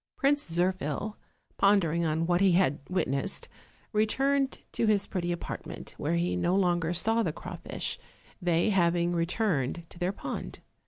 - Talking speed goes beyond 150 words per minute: No, average, 145 wpm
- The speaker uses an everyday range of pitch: Yes, average, 3.3 semitones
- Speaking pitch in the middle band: Yes, medium, 175 Hz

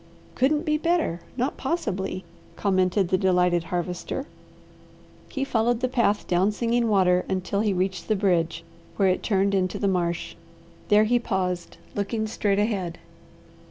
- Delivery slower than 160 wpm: Yes, average, 145 wpm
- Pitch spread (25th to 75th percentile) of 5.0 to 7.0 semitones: No, average, 4.0 semitones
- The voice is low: No, high, 195 Hz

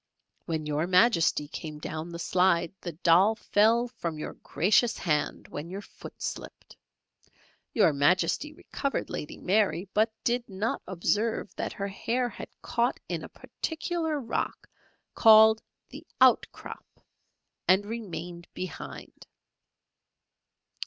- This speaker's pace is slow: Yes, slow, 120 wpm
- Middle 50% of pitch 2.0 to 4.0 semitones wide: No, average, 5.2 semitones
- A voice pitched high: Yes, high, 195 Hz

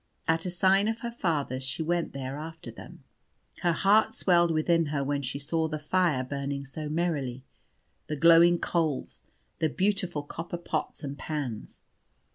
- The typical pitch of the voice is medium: Yes, medium, 160 Hz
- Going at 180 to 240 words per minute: No, average, 160 wpm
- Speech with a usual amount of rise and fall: Yes, average, 3.6 semitones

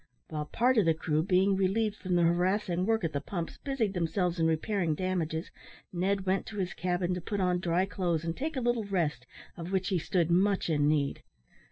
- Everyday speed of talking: No, fast, 210 wpm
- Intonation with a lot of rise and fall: No, average, 3.0 semitones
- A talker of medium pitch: Yes, medium, 180 Hz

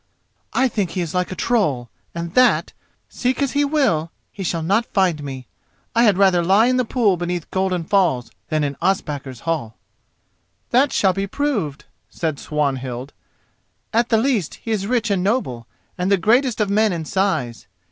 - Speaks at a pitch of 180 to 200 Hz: Yes, high, 190 Hz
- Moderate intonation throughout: No, wide, 6.4 semitones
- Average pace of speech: Yes, average, 175 wpm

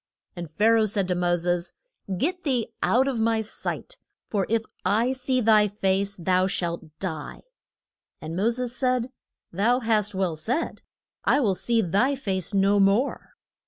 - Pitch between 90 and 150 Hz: No, high, 210 Hz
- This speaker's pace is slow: No, average, 165 wpm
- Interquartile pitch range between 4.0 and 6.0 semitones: Yes, average, 4.5 semitones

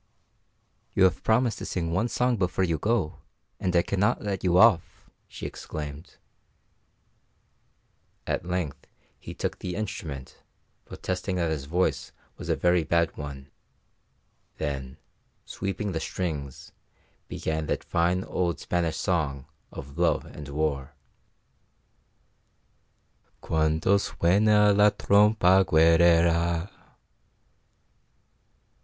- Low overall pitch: Yes, very low, 85 Hz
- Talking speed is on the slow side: Yes, slow, 110 wpm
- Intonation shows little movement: No, average, 3.6 semitones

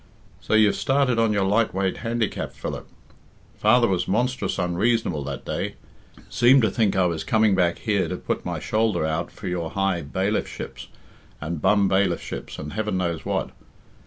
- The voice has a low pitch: Yes, low, 100 Hz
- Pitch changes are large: No, average, 3.9 semitones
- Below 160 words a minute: No, average, 165 wpm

